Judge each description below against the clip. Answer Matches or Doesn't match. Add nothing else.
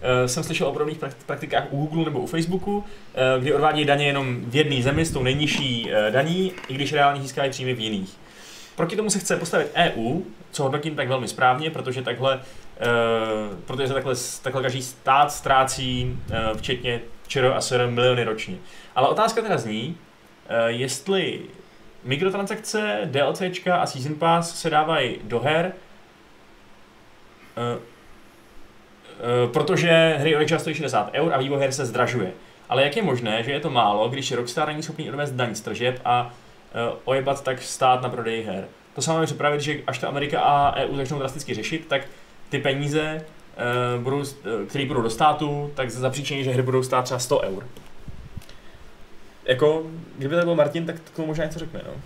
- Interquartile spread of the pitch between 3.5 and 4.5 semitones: Matches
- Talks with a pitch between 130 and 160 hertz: Matches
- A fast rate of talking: Matches